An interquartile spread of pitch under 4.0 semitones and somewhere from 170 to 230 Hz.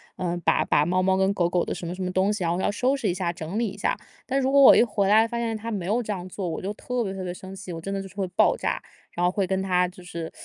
Yes: average, 2.9 semitones; high, 190 Hz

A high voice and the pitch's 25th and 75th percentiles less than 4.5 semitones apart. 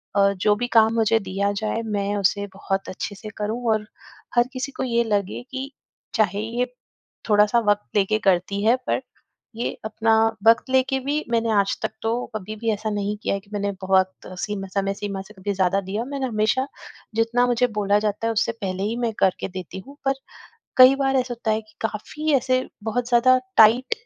Yes: high, 215 Hz; average, 3.2 semitones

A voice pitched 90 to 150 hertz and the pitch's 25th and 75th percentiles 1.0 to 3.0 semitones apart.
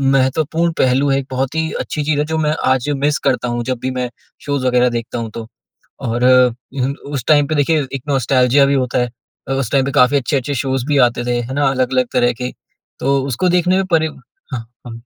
Yes: low, 135 Hz; narrow, 2.6 semitones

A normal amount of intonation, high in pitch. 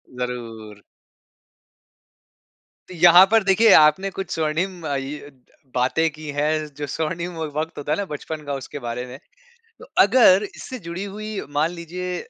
No: average, 4.2 semitones; medium, 160 Hz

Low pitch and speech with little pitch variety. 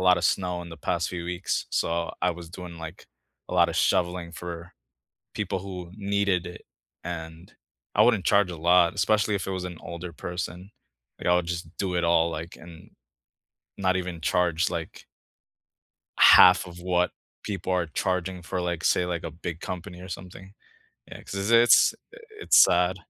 Yes: very low, 90 Hz; narrow, 1.4 semitones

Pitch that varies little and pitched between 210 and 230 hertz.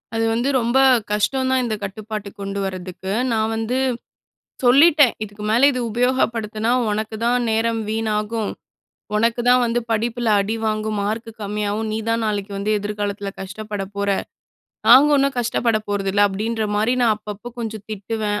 Yes: narrow, 2.2 semitones; high, 220 Hz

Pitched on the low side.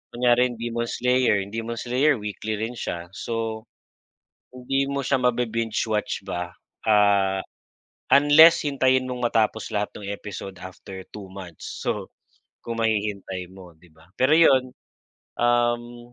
Yes: low, 115 Hz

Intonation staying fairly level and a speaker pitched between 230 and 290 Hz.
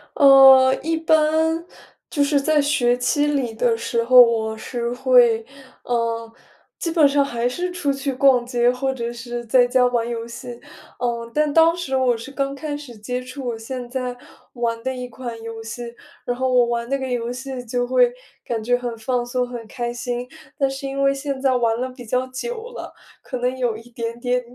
Yes: narrow, 2.3 semitones; very high, 250 Hz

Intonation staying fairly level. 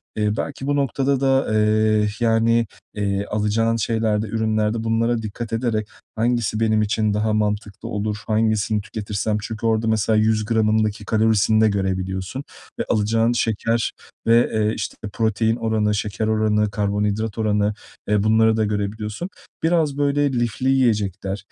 Yes: narrow, 1.4 semitones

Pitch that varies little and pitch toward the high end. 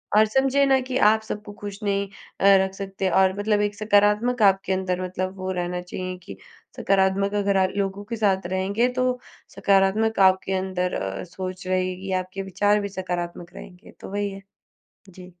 Yes: narrow, 1.8 semitones; high, 195 Hz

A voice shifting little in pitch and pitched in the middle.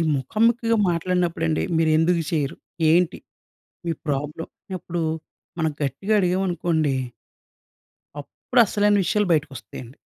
No: average, 3.6 semitones; medium, 165 Hz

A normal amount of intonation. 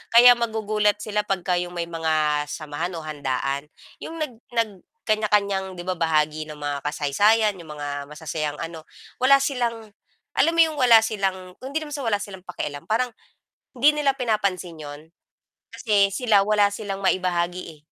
No: wide, 5.7 semitones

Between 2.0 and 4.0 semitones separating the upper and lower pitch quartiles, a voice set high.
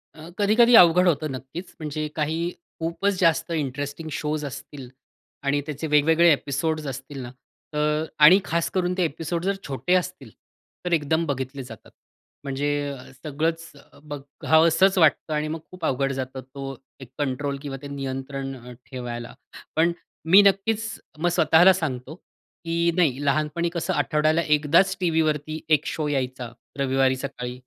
No: average, 3.4 semitones; medium, 150 Hz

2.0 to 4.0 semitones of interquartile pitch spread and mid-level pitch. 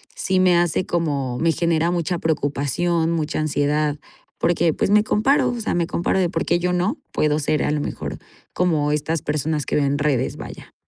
Yes: average, 2.8 semitones; medium, 165 Hz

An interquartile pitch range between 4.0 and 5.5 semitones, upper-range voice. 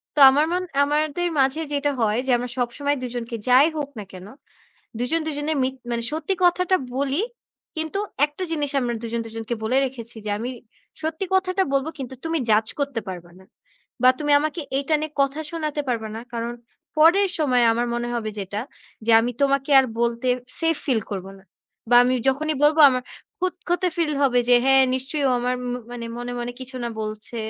Yes: average, 4.5 semitones; very high, 265 Hz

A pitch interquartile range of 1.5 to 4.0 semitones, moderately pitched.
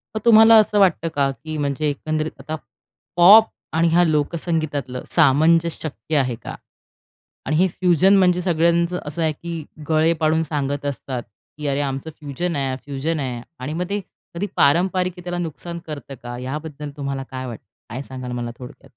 Yes: average, 3.7 semitones; medium, 155 Hz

